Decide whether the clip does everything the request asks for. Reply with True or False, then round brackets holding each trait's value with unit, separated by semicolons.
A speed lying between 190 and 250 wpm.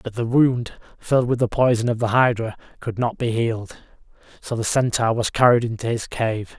True (200 wpm)